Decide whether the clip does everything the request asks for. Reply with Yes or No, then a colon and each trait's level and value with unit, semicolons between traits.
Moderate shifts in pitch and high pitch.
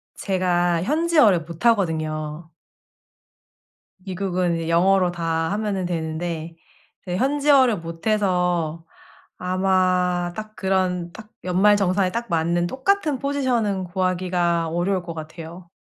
No: average, 3.2 semitones; medium, 180 Hz